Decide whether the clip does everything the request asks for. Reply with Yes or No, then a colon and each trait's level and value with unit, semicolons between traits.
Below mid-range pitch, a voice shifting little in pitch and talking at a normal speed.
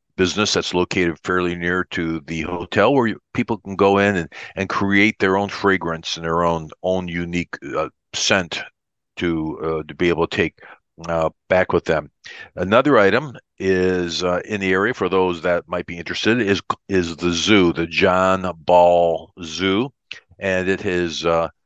Yes: very low, 90 Hz; narrow, 2.2 semitones; average, 175 wpm